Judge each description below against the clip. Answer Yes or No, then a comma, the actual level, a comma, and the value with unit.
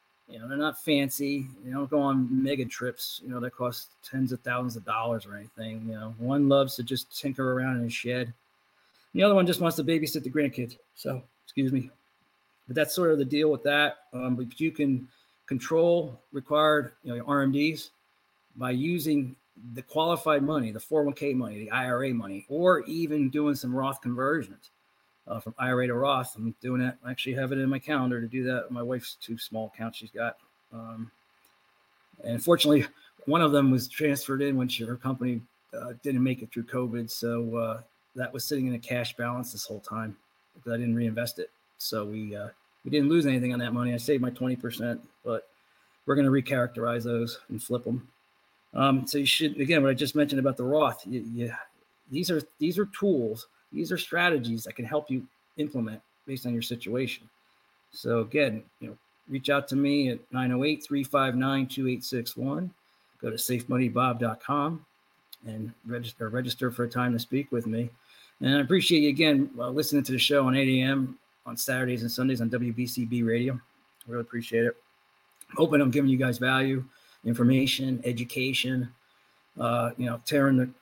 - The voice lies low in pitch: Yes, low, 130 Hz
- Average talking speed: Yes, average, 190 wpm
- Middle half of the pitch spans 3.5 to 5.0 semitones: No, narrow, 2.5 semitones